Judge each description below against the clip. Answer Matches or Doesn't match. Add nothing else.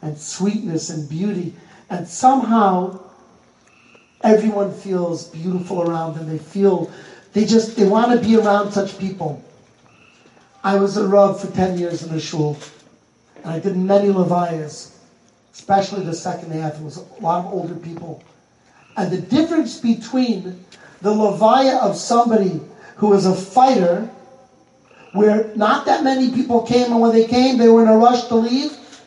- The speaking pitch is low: Doesn't match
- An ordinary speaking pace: Matches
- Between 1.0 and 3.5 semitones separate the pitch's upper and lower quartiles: Doesn't match